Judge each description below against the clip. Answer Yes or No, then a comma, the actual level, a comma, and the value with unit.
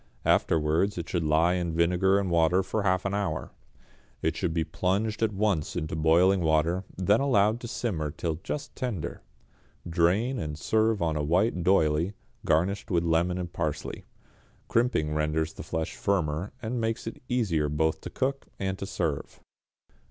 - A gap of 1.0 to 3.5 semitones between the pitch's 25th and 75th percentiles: No, average, 4.3 semitones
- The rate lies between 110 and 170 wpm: Yes, average, 165 wpm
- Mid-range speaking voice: No, very low, 90 Hz